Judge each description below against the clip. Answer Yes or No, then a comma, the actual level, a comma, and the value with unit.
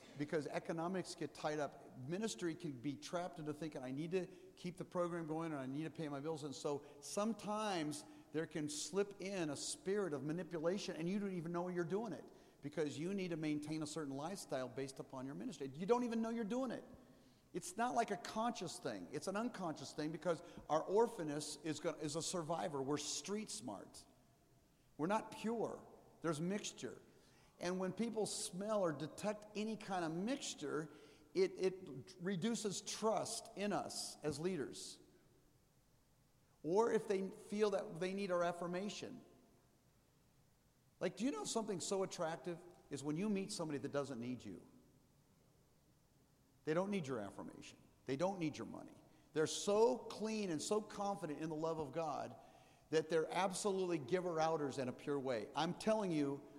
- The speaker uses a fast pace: No, average, 175 wpm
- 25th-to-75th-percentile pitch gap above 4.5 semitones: Yes, average, 4.9 semitones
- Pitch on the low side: No, medium, 175 Hz